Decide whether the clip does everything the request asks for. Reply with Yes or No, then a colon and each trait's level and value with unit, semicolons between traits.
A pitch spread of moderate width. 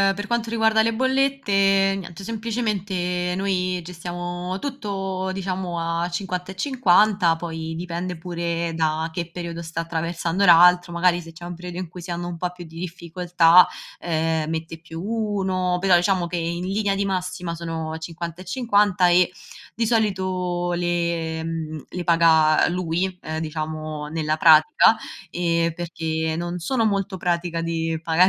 No: narrow, 2.3 semitones